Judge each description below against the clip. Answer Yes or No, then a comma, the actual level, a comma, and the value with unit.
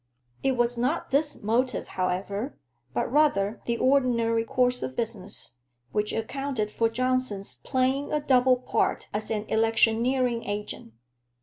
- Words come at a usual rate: No, slow, 130 wpm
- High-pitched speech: Yes, high, 235 Hz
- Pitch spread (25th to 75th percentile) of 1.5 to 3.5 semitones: Yes, average, 3.2 semitones